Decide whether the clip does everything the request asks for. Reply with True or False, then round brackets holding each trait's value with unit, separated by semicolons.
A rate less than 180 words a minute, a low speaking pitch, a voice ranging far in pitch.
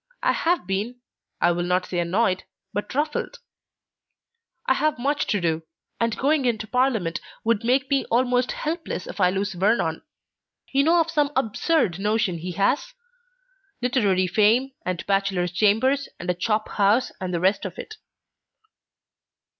False (155 wpm; 215 Hz; 6.3 semitones)